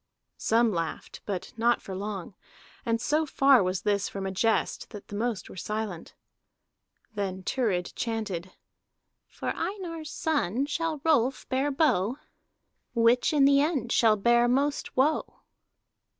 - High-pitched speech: Yes, high, 230 Hz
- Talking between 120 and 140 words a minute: Yes, slow, 135 wpm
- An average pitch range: No, wide, 5.7 semitones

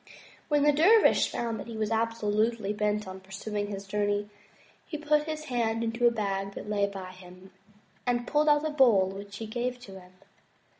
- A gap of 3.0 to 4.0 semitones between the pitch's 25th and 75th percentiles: Yes, average, 3.7 semitones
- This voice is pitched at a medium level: No, high, 215 Hz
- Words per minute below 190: No, average, 195 wpm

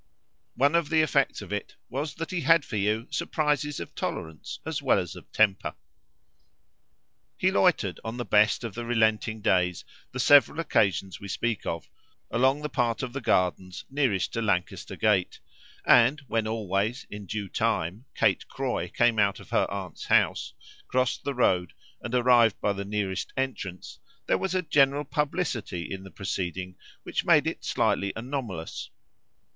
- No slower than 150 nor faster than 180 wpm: Yes, average, 165 wpm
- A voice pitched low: Yes, low, 115 Hz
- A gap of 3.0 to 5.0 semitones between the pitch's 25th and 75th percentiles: No, wide, 5.6 semitones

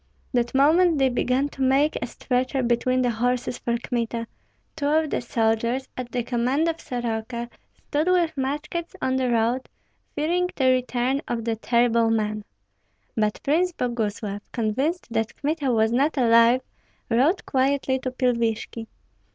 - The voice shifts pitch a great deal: No, average, 3.2 semitones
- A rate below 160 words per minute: Yes, average, 150 wpm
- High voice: Yes, very high, 250 Hz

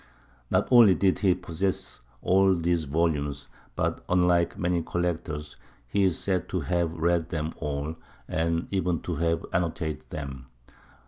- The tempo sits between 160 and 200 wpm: No, average, 140 wpm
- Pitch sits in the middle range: No, very low, 85 Hz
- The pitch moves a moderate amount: No, narrow, 2.3 semitones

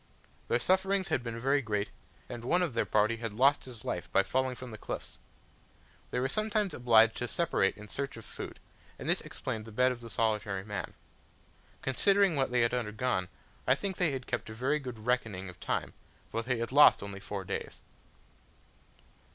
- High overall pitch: No, low, 120 Hz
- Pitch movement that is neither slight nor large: Yes, average, 3.9 semitones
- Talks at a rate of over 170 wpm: Yes, average, 190 wpm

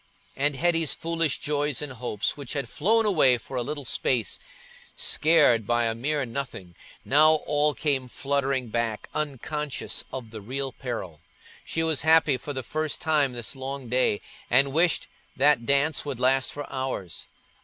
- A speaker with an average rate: Yes, average, 160 wpm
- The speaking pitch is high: No, medium, 140 Hz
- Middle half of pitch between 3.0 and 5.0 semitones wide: Yes, average, 3.3 semitones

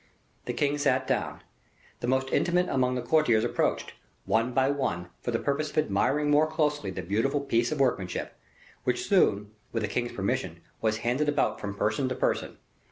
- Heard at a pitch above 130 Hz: No, low, 125 Hz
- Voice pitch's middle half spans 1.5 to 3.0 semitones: No, average, 4.8 semitones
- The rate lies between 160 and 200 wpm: Yes, average, 180 wpm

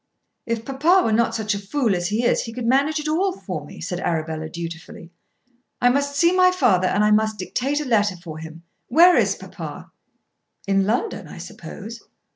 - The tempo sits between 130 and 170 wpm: No, average, 195 wpm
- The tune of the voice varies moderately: No, wide, 7.4 semitones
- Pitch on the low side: No, high, 225 Hz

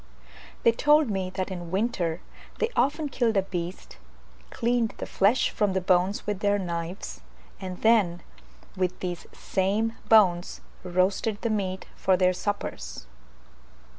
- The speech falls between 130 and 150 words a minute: Yes, slow, 135 wpm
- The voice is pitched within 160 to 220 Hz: Yes, high, 190 Hz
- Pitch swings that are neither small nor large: Yes, average, 3.5 semitones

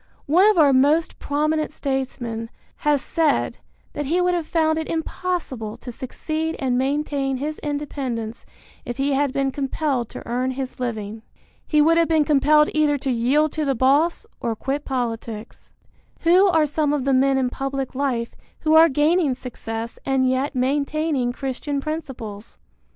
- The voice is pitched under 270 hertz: No, very high, 275 Hz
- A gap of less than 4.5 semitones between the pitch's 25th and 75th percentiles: Yes, average, 3.2 semitones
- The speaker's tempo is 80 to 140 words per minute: No, average, 160 wpm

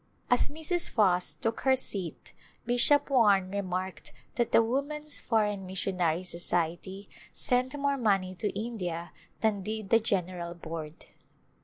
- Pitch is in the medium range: No, high, 200 Hz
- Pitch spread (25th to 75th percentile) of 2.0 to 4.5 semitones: No, average, 5.1 semitones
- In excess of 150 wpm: No, slow, 135 wpm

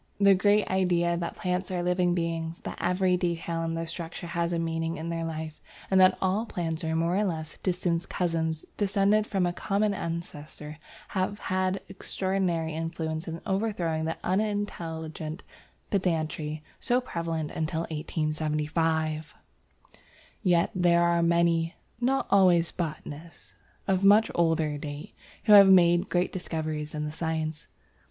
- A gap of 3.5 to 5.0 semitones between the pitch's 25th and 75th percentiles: No, narrow, 2.5 semitones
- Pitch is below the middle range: No, medium, 170 Hz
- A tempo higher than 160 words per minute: No, average, 140 wpm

